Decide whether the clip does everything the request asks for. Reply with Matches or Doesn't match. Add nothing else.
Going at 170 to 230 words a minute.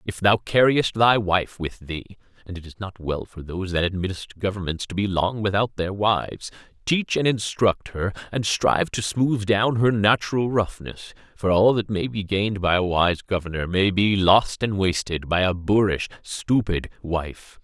Matches